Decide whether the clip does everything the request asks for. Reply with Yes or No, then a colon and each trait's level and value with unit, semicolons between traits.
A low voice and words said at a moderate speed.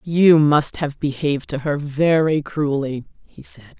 No: medium, 145 Hz; average, 160 wpm